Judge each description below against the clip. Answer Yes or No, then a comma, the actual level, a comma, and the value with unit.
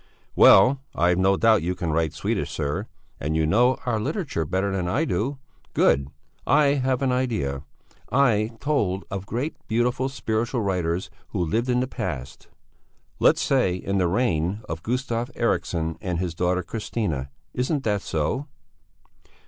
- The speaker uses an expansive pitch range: Yes, wide, 6.5 semitones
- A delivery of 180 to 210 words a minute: No, average, 155 wpm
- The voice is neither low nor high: No, low, 100 Hz